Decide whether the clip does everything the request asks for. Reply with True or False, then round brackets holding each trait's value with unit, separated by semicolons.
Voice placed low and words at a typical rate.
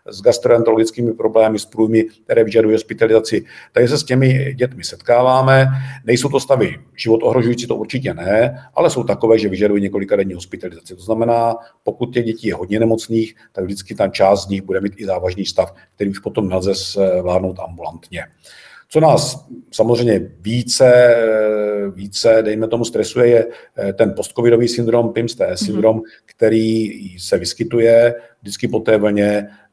True (110 Hz; 145 wpm)